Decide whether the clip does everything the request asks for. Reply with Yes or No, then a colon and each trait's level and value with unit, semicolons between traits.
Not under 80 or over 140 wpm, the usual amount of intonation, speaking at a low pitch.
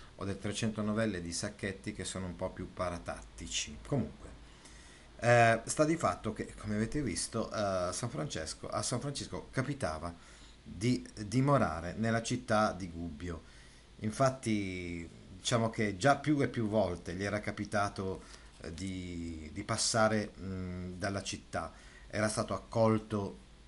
Yes: average, 135 wpm; average, 3.8 semitones; low, 105 Hz